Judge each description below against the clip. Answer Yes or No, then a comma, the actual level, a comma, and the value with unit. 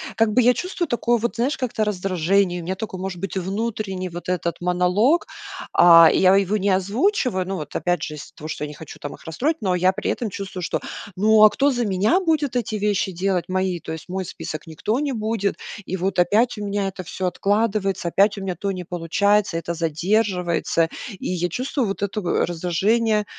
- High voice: Yes, high, 195 Hz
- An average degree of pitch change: Yes, average, 3.5 semitones